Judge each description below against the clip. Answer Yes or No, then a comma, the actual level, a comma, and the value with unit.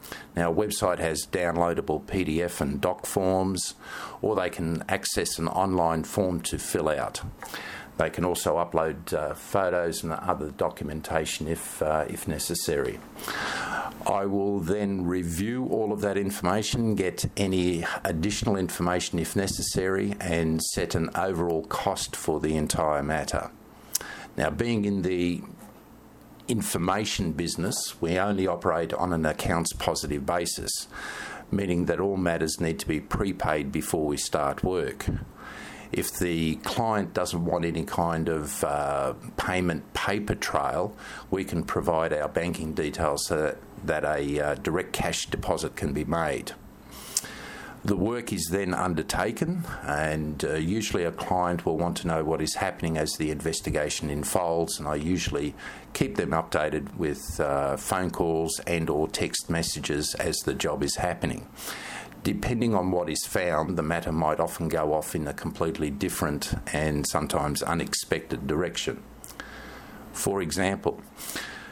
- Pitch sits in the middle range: No, very low, 85 Hz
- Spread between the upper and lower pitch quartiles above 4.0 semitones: No, average, 3.3 semitones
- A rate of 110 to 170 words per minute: Yes, average, 140 wpm